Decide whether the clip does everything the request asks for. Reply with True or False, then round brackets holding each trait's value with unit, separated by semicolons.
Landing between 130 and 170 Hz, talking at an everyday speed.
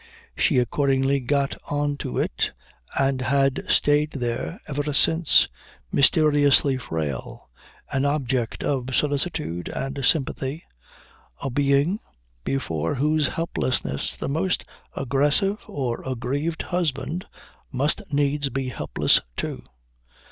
False (140 Hz; 105 wpm)